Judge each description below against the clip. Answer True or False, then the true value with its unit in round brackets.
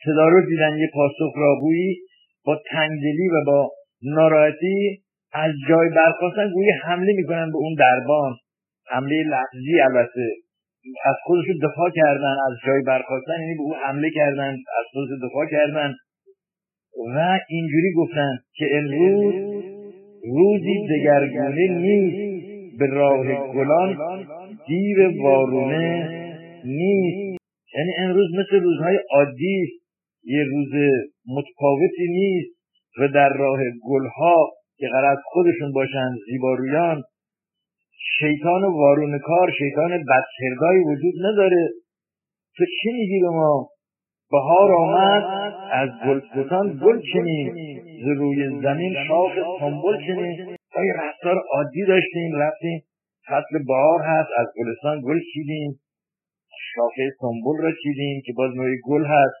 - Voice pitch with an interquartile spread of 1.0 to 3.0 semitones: False (4.7 semitones)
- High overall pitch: False (160 Hz)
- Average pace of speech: True (115 wpm)